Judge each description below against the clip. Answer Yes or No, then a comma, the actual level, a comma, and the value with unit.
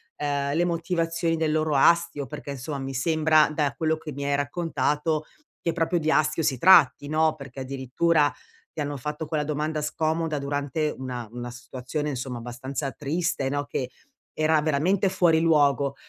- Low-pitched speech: No, medium, 150 Hz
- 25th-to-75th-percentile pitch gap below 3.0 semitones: Yes, narrow, 2.5 semitones